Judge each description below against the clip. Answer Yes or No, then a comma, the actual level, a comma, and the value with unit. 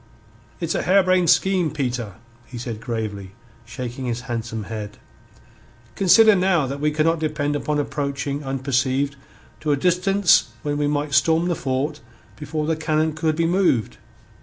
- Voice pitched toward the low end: No, medium, 145 Hz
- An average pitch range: Yes, average, 4.3 semitones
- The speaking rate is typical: Yes, average, 150 wpm